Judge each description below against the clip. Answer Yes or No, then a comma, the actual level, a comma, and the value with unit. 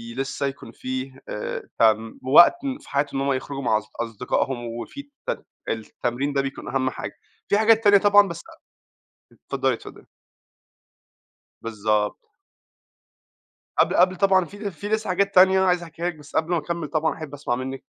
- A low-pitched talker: No, medium, 145 Hz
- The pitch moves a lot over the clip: Yes, wide, 6.4 semitones